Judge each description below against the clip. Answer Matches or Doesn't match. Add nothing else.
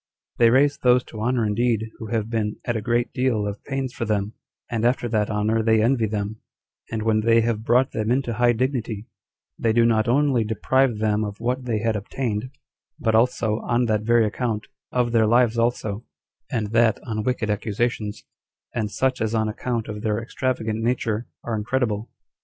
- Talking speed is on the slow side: Doesn't match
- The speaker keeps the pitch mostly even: Matches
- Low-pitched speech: Matches